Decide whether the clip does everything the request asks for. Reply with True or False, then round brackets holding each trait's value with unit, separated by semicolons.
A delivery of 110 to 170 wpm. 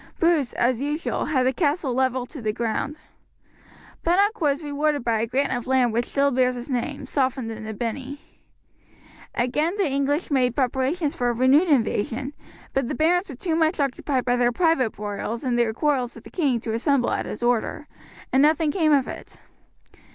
False (185 wpm)